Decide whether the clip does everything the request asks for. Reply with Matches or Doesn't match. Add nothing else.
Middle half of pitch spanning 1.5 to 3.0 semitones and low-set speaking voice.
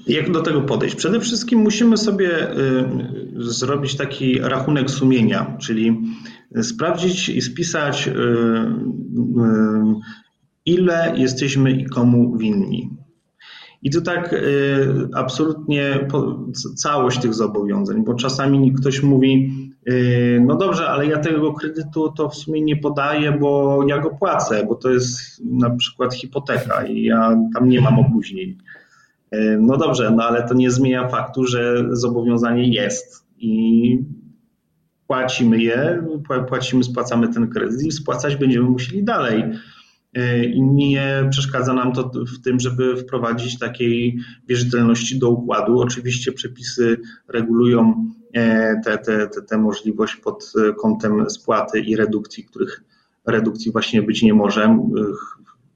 Doesn't match